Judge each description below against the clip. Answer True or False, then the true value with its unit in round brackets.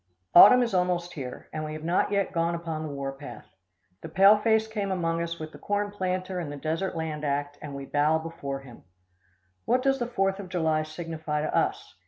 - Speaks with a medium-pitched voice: True (165 Hz)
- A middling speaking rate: False (215 wpm)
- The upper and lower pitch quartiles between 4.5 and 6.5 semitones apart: False (4.0 semitones)